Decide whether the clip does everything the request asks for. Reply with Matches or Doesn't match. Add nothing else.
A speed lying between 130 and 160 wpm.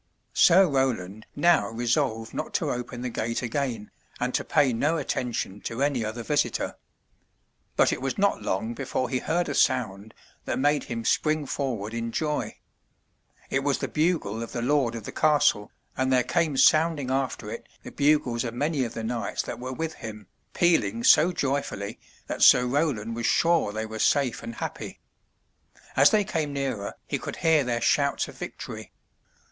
Doesn't match